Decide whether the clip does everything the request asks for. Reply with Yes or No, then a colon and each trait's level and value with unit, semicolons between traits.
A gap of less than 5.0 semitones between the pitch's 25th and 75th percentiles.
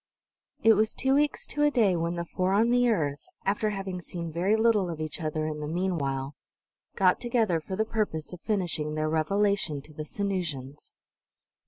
No: wide, 5.4 semitones